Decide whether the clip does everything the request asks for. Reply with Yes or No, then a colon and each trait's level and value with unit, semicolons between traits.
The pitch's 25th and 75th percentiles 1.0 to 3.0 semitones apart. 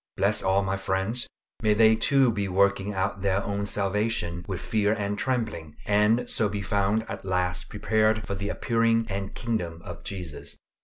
Yes: narrow, 2.4 semitones